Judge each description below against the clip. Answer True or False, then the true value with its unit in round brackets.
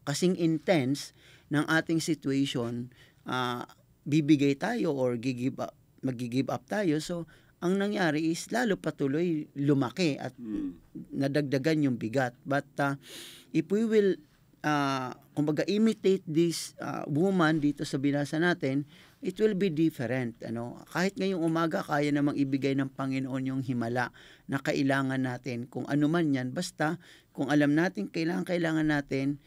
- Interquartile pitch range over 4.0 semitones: False (3.5 semitones)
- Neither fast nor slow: True (135 wpm)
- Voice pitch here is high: False (150 Hz)